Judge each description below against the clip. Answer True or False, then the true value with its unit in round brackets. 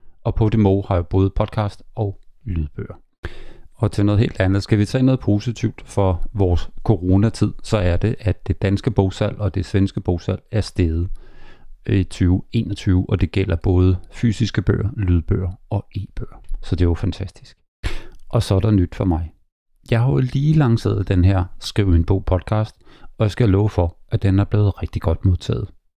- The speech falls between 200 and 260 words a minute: False (190 wpm)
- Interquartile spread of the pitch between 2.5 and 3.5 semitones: True (2.9 semitones)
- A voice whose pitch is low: True (100 Hz)